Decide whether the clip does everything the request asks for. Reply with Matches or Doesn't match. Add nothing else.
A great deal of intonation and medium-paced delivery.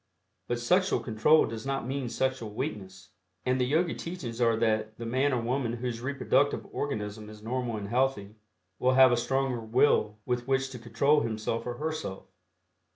Doesn't match